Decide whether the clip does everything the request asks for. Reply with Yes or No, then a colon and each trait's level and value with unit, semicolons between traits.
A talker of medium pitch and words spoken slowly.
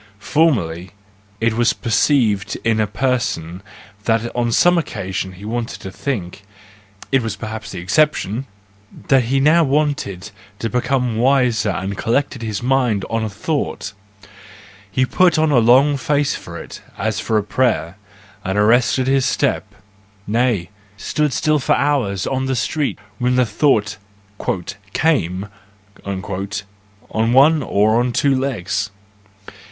No: low, 115 Hz; slow, 130 wpm